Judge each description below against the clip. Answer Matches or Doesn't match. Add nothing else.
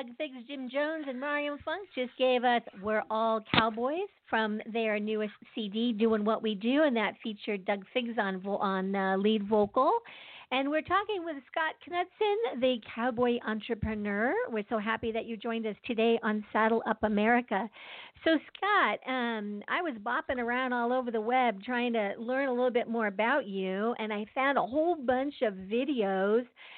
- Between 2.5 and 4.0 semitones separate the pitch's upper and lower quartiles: Matches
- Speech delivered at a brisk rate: Doesn't match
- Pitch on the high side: Matches